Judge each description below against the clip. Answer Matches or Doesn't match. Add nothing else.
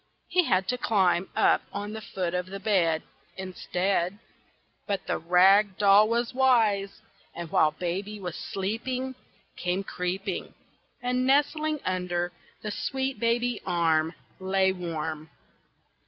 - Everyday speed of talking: Doesn't match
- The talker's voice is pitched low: Doesn't match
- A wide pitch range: Doesn't match